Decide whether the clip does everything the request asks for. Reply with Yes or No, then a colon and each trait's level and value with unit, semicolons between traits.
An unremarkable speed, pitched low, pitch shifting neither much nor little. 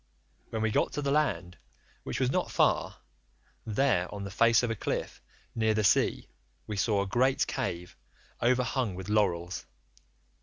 Yes: average, 160 wpm; low, 110 Hz; average, 4.3 semitones